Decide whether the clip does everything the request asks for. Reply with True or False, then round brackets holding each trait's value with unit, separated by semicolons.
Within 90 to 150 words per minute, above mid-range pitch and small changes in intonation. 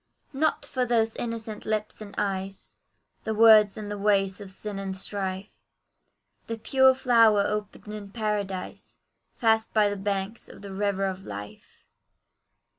True (145 wpm; 210 Hz; 2.2 semitones)